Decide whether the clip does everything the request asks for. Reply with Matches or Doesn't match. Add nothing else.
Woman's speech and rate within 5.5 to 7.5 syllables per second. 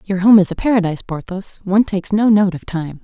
Matches